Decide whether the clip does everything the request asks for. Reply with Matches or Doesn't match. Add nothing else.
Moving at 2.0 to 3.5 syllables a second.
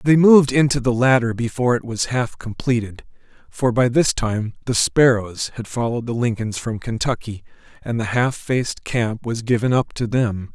Doesn't match